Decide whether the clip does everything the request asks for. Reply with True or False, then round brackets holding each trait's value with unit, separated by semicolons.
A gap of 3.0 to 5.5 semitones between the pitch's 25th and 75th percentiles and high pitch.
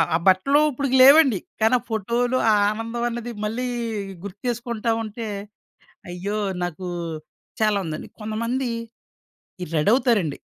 True (3.3 semitones; 230 Hz)